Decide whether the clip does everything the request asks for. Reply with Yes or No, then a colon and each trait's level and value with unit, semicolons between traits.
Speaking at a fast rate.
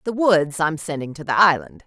Yes: fast, 225 wpm